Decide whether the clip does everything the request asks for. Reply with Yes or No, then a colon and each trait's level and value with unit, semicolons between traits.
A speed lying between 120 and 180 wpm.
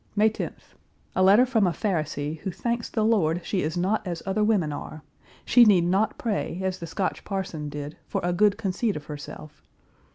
No: average, 195 wpm